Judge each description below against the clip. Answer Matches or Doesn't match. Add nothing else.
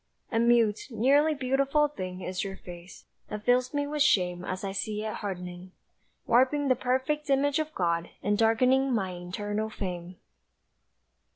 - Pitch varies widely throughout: Matches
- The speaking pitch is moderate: Doesn't match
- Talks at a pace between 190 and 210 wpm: Doesn't match